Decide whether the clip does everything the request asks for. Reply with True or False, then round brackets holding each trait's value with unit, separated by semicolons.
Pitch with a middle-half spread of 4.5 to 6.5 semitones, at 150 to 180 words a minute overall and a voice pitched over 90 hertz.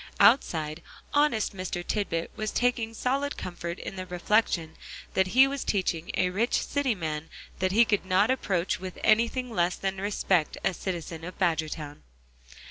True (4.8 semitones; 155 wpm; 190 Hz)